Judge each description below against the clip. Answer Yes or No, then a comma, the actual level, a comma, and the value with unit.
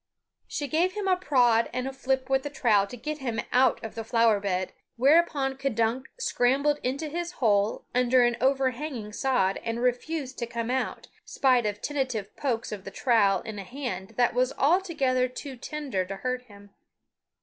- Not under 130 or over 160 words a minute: No, average, 180 wpm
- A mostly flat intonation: No, average, 3.5 semitones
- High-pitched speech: Yes, very high, 255 Hz